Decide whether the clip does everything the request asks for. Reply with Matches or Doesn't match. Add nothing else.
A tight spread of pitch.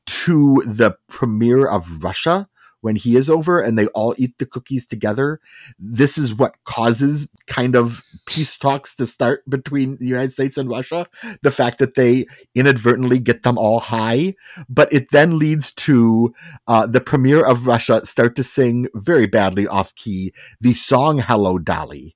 Doesn't match